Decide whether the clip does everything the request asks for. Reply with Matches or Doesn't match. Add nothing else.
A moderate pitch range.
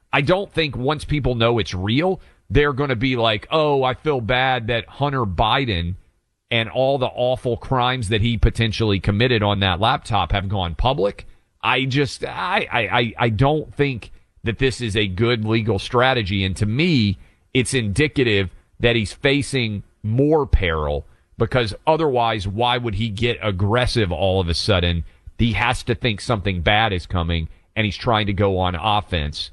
Matches